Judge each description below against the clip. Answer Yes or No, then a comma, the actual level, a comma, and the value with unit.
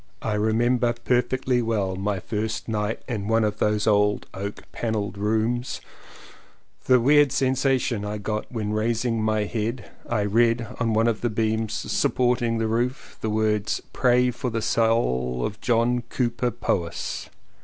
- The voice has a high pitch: No, low, 115 Hz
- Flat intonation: Yes, narrow, 2.3 semitones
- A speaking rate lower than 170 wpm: Yes, average, 155 wpm